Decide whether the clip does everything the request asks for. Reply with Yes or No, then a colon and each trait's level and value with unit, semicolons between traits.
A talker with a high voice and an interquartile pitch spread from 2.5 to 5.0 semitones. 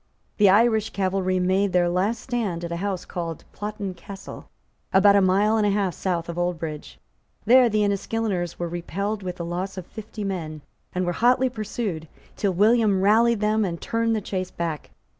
Yes: high, 195 Hz; average, 3.4 semitones